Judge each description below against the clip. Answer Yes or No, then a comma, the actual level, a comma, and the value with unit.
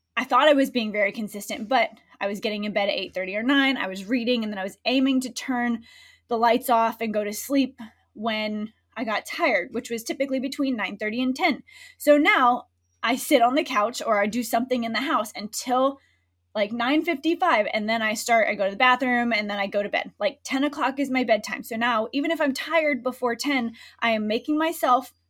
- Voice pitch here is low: No, high, 245 Hz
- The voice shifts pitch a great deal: No, average, 4.3 semitones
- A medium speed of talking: No, fast, 225 wpm